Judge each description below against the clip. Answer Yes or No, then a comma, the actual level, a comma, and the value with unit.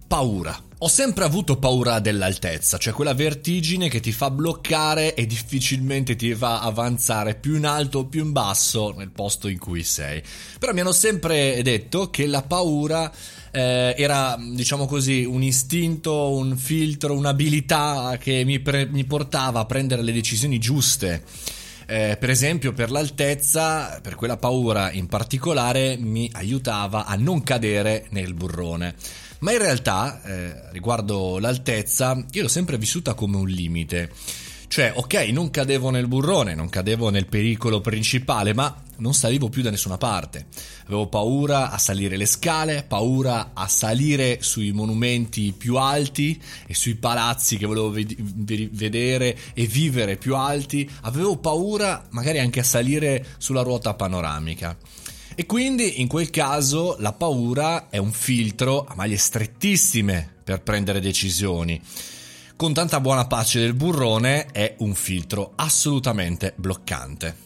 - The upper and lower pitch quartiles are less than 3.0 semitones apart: No, average, 5.3 semitones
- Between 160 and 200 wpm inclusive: No, average, 145 wpm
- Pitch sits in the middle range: No, low, 120 Hz